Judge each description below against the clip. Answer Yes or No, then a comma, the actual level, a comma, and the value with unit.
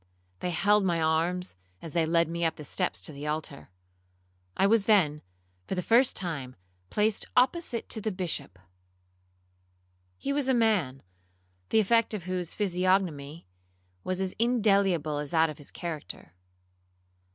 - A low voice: No, medium, 180 Hz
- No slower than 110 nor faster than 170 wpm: Yes, average, 150 wpm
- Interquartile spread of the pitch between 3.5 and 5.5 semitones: Yes, average, 4.8 semitones